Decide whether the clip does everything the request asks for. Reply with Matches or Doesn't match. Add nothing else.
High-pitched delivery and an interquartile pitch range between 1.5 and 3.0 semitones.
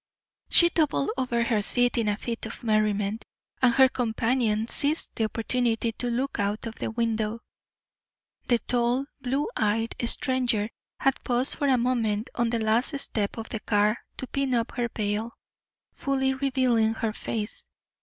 Matches